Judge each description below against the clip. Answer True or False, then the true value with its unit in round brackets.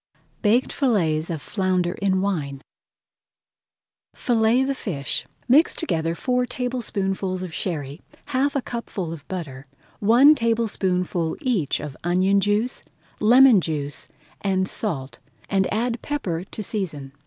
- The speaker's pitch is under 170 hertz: False (195 Hz)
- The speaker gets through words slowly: True (130 wpm)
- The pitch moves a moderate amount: False (6.0 semitones)